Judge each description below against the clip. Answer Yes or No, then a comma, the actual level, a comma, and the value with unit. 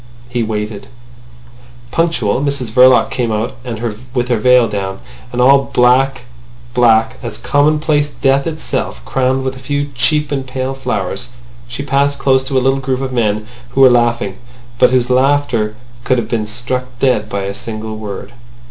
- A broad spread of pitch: No, average, 3.1 semitones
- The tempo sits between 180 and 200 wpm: No, average, 160 wpm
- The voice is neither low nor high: No, low, 125 Hz